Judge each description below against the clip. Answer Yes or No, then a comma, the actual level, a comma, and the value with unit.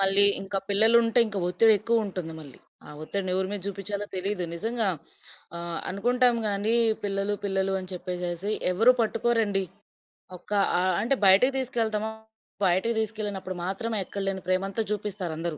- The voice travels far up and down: No, average, 2.9 semitones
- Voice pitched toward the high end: Yes, high, 200 Hz